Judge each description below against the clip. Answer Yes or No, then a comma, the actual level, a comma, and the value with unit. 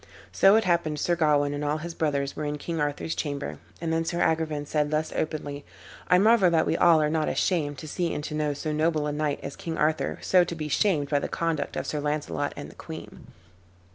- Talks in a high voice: No, medium, 155 Hz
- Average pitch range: No, narrow, 2.1 semitones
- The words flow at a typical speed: No, fast, 230 wpm